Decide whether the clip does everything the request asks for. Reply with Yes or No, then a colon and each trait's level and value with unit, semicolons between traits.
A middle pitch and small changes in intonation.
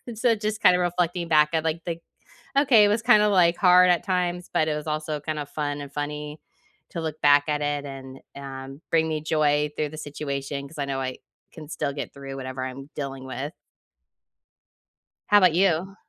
No: medium, 150 Hz; average, 3.8 semitones